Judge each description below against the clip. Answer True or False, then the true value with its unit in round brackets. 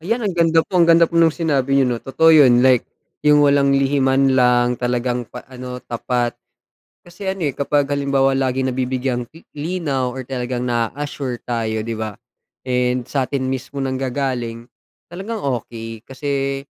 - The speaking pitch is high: False (135 Hz)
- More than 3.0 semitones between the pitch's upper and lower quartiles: False (2.7 semitones)